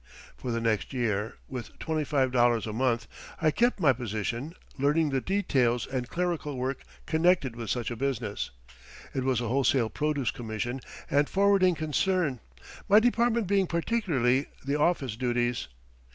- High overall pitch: No, low, 135 Hz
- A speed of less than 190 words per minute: Yes, average, 145 wpm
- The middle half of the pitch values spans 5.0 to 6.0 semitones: Yes, wide, 5.4 semitones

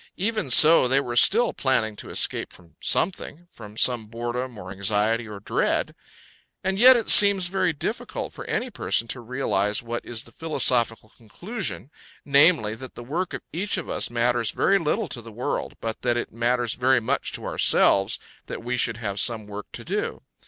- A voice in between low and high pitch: No, low, 120 Hz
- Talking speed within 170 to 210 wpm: Yes, average, 185 wpm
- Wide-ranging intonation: Yes, wide, 6.4 semitones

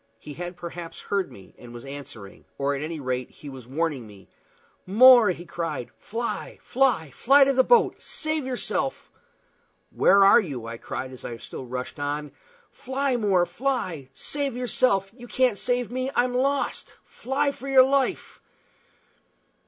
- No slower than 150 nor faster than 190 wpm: Yes, average, 160 wpm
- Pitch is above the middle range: Yes, high, 195 Hz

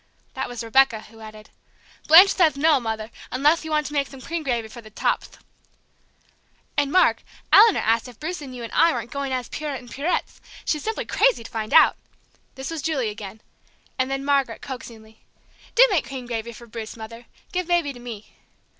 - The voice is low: No, very high, 265 Hz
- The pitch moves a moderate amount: Yes, average, 4.9 semitones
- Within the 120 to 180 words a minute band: No, average, 195 wpm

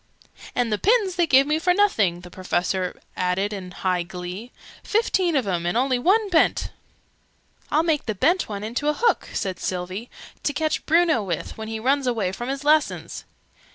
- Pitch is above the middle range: Yes, high, 240 Hz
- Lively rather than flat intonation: Yes, wide, 9.0 semitones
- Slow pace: No, average, 185 wpm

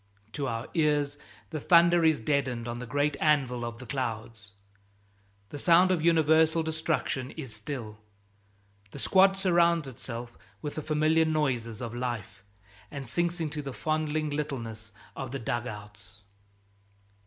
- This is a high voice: No, medium, 140 Hz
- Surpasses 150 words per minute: No, average, 140 wpm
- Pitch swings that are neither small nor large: Yes, average, 5.0 semitones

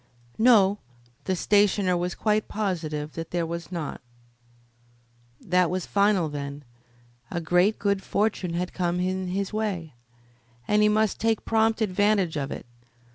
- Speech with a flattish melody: No, average, 3.5 semitones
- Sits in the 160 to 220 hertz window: Yes, medium, 185 Hz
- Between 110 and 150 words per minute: Yes, average, 140 wpm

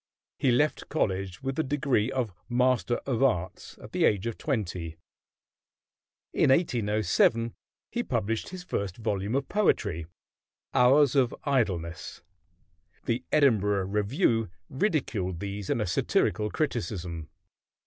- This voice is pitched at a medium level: No, low, 115 Hz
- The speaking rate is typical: No, slow, 120 wpm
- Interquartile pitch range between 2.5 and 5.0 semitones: No, wide, 5.4 semitones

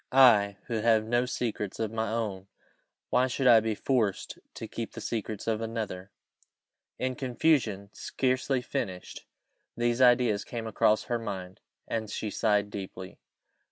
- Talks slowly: No, average, 145 wpm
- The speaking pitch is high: No, low, 110 Hz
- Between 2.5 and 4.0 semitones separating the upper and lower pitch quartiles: Yes, average, 3.0 semitones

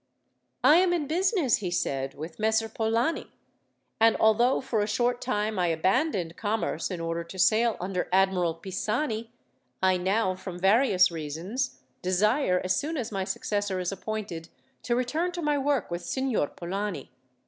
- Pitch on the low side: No, high, 210 Hz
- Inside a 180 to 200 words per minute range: No, average, 160 wpm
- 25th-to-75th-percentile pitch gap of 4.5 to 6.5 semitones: Yes, average, 5.1 semitones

